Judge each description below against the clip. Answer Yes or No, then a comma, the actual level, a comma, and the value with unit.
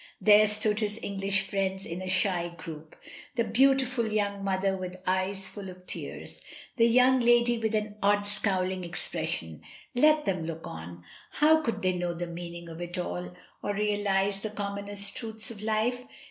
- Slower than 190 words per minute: Yes, average, 175 wpm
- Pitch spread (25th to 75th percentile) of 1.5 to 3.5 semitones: Yes, average, 3.0 semitones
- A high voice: Yes, high, 200 Hz